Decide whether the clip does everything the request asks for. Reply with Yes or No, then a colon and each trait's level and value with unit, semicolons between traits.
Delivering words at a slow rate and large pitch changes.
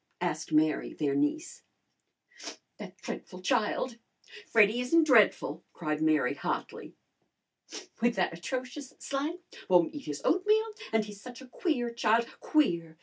Yes: slow, 130 wpm; wide, 8.2 semitones